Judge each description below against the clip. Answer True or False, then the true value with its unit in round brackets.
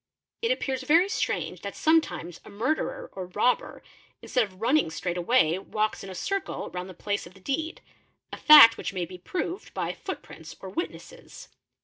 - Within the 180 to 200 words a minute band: True (185 wpm)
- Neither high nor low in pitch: False (230 Hz)